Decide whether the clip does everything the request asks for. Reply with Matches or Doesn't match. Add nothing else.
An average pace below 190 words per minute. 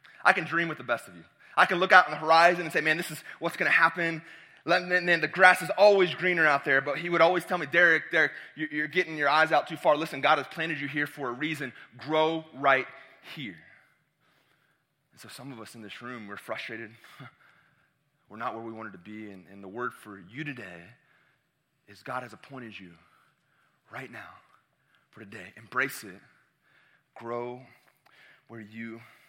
Doesn't match